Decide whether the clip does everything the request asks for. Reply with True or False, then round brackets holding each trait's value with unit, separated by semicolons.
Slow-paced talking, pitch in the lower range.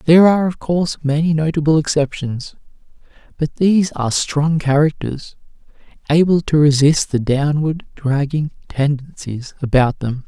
False (125 wpm; 150 Hz)